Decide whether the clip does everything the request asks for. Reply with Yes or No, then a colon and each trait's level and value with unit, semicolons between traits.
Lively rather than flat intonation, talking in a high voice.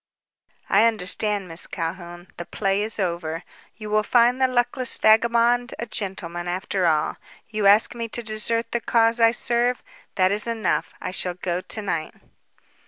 No: average, 4.3 semitones; high, 215 Hz